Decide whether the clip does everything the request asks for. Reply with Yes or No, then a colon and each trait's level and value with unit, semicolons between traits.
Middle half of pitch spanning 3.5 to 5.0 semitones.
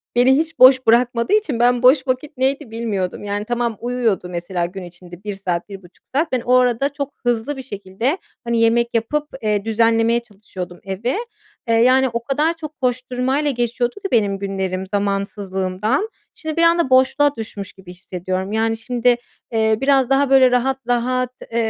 Yes: average, 4.5 semitones